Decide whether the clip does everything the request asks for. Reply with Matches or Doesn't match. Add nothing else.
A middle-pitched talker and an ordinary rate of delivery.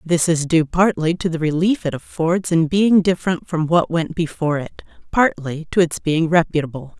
Matches